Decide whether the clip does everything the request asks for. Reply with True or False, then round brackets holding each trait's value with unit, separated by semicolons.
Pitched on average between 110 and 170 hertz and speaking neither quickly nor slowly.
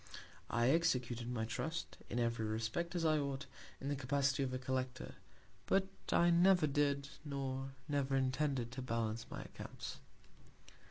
True (135 Hz; 150 wpm)